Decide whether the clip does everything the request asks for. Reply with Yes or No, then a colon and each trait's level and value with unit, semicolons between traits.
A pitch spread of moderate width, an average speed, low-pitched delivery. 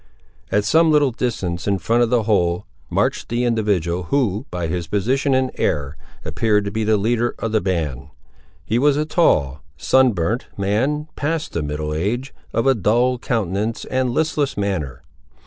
No: wide, 6.2 semitones; average, 170 wpm; low, 110 Hz